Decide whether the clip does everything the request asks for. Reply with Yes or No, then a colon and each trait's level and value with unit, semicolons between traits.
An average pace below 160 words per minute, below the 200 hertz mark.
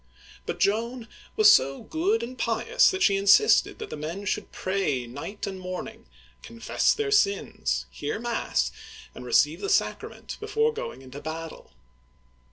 No: average, 150 wpm; high, 205 Hz